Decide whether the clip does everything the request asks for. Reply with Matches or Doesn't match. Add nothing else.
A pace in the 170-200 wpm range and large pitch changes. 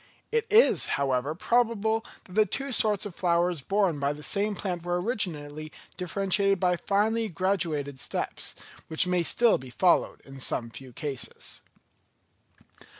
Doesn't match